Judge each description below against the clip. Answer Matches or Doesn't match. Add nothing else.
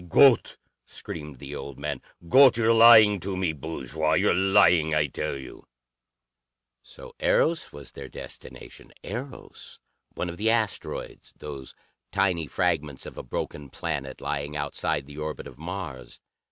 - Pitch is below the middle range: Matches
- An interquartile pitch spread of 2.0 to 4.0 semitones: Doesn't match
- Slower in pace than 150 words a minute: Matches